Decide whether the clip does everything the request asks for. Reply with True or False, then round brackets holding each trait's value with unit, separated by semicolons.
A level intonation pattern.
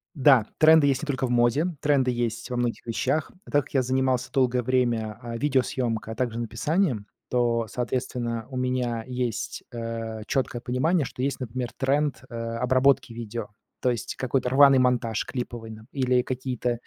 True (2.2 semitones)